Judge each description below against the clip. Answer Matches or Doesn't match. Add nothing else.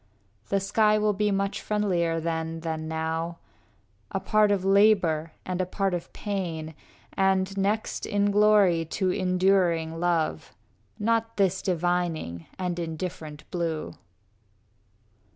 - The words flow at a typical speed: Doesn't match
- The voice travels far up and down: Doesn't match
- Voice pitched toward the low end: Doesn't match